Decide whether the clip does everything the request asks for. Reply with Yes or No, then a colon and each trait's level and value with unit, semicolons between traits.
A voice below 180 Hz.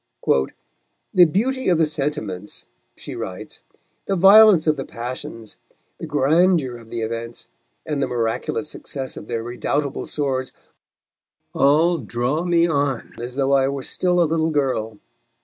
Yes: medium, 140 Hz